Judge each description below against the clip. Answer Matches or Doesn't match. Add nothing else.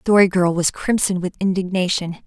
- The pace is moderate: Matches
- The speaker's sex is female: Matches